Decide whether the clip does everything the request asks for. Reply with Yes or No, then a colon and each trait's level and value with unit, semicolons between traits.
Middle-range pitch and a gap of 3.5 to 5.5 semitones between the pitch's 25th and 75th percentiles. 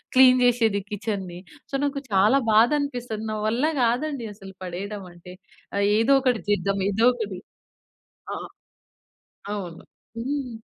No: high, 220 Hz; average, 4.1 semitones